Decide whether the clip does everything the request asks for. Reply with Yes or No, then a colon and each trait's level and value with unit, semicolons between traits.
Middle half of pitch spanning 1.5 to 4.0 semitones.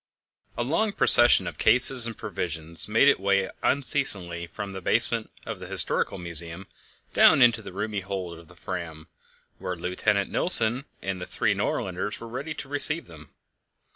No: wide, 5.6 semitones